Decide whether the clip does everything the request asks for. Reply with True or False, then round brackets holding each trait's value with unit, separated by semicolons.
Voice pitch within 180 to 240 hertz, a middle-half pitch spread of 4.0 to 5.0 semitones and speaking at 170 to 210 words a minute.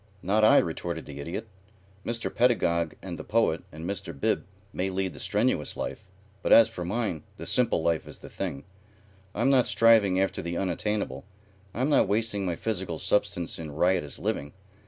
False (95 Hz; 4.7 semitones; 175 wpm)